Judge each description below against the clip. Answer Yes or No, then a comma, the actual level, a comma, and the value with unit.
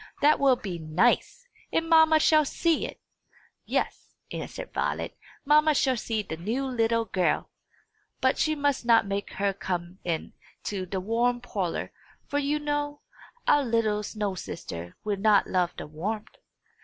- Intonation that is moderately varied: No, wide, 7.0 semitones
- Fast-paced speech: No, average, 150 wpm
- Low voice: No, high, 225 Hz